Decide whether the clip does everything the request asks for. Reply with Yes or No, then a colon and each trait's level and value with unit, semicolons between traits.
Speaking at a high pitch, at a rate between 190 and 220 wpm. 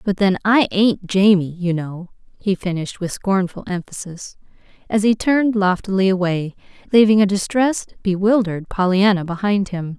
No: high, 195 Hz; average, 145 wpm